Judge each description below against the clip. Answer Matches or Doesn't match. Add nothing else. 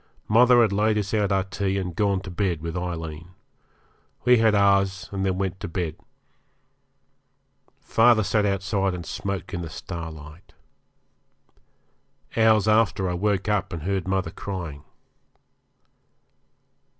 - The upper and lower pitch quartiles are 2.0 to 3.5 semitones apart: Matches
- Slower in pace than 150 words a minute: Matches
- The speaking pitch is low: Matches